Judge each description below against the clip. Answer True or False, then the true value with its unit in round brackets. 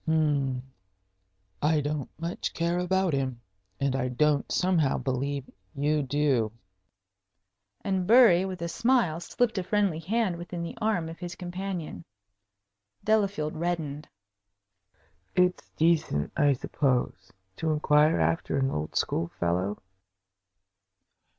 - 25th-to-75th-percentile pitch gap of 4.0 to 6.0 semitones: True (4.5 semitones)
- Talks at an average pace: False (120 wpm)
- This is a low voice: False (160 Hz)